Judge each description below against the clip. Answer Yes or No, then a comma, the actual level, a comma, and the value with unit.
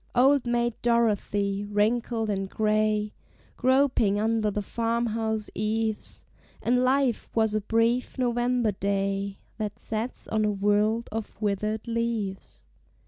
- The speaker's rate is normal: No, slow, 125 wpm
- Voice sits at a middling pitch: No, high, 220 Hz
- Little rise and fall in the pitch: Yes, narrow, 2.2 semitones